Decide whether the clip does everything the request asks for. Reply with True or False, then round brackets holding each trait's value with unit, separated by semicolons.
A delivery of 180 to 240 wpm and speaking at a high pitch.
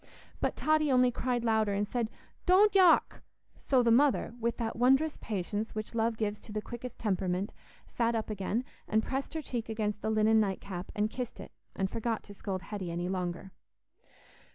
True (185 wpm; 220 Hz)